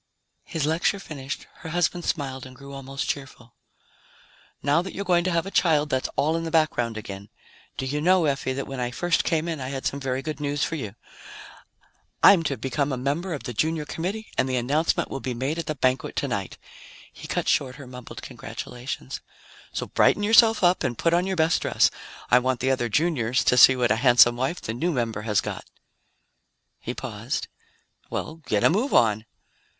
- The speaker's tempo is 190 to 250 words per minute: Yes, average, 200 wpm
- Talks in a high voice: No, medium, 140 Hz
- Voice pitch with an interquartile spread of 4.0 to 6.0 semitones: Yes, average, 4.5 semitones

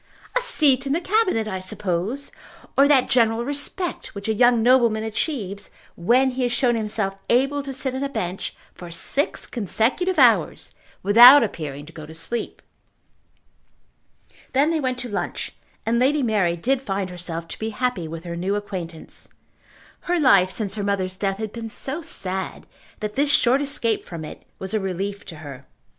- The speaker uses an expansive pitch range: Yes, wide, 5.8 semitones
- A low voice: No, high, 220 Hz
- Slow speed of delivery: No, average, 175 wpm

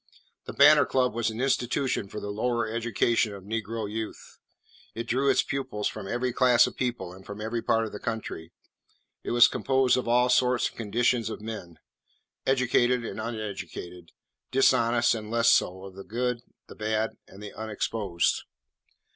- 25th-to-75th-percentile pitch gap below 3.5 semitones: Yes, narrow, 2.6 semitones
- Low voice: Yes, low, 115 Hz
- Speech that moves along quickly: No, average, 170 wpm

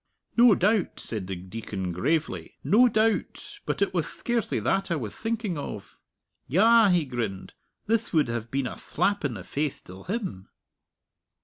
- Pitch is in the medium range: Yes, medium, 155 Hz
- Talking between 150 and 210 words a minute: Yes, average, 165 wpm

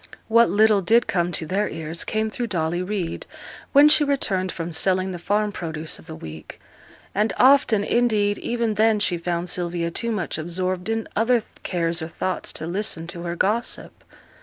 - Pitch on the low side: No, high, 190 Hz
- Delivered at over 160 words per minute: Yes, average, 180 wpm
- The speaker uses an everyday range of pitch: Yes, average, 4.3 semitones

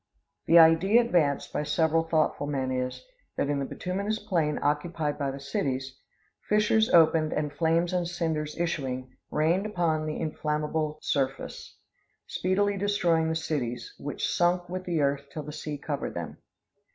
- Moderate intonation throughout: Yes, average, 3.2 semitones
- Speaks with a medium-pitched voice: Yes, medium, 160 Hz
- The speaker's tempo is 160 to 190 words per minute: No, average, 150 wpm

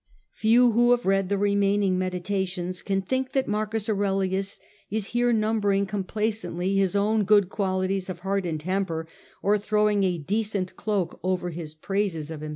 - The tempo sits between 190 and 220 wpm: No, average, 165 wpm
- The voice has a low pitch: No, high, 195 Hz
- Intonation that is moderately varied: No, narrow, 2.3 semitones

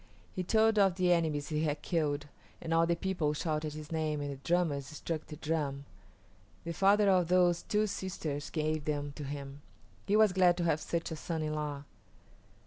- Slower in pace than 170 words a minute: No, average, 195 wpm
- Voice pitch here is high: No, medium, 160 Hz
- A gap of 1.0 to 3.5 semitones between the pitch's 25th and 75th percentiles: Yes, average, 3.2 semitones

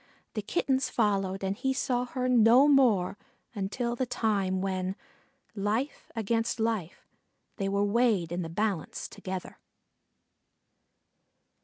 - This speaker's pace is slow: Yes, slow, 120 wpm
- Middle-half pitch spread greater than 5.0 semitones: No, average, 4.0 semitones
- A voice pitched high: Yes, high, 215 Hz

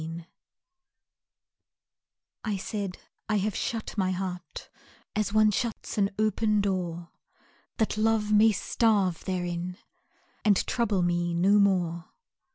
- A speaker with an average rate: No, slow, 115 wpm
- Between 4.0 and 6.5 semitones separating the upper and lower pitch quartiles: No, average, 3.2 semitones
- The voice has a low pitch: No, high, 195 Hz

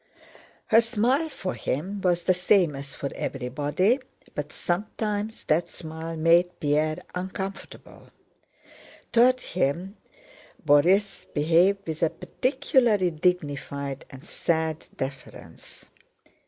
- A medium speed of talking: No, slow, 100 wpm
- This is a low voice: No, medium, 175 Hz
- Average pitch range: Yes, average, 5.0 semitones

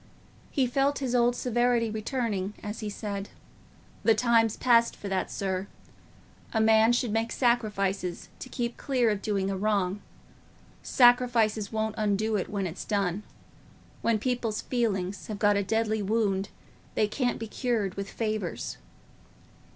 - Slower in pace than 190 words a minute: Yes, average, 145 wpm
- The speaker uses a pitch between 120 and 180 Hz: No, high, 220 Hz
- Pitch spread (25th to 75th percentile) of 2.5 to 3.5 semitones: Yes, average, 2.9 semitones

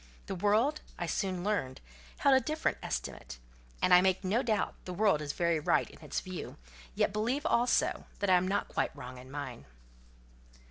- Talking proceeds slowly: No, average, 185 wpm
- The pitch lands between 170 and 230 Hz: Yes, high, 190 Hz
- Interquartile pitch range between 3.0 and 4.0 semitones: No, average, 4.9 semitones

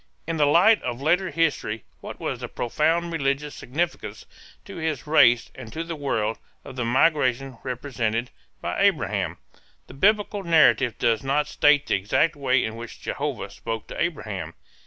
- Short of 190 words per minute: Yes, average, 160 wpm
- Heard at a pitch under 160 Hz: Yes, medium, 140 Hz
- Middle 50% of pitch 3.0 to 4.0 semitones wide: No, wide, 5.5 semitones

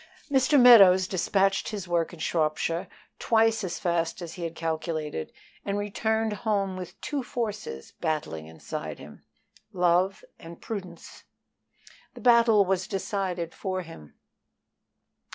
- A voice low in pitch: No, medium, 185 Hz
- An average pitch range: Yes, average, 3.9 semitones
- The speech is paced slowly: Yes, slow, 125 wpm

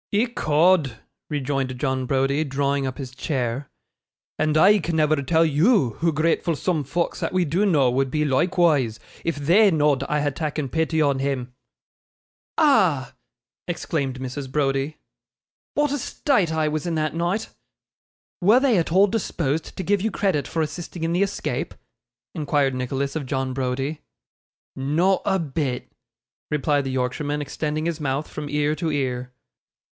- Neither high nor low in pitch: Yes, medium, 150 Hz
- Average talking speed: Yes, average, 155 wpm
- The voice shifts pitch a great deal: No, average, 3.8 semitones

